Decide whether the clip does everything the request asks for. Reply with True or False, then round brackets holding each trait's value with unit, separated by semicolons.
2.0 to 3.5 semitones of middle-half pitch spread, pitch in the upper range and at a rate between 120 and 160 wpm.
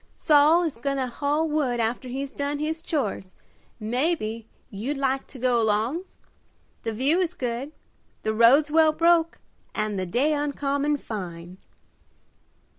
False (4.8 semitones; 275 Hz; 140 wpm)